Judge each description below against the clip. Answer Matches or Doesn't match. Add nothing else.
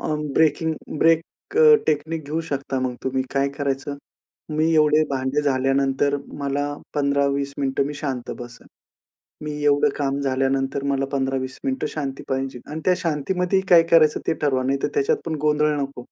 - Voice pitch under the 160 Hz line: Matches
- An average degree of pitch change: Doesn't match